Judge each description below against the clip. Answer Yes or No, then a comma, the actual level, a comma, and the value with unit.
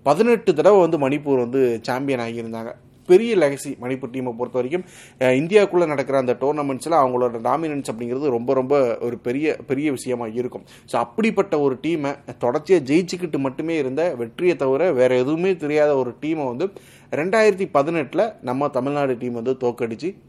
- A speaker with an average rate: No, fast, 150 wpm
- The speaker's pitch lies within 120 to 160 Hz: Yes, low, 135 Hz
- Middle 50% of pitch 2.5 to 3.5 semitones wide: No, average, 4.6 semitones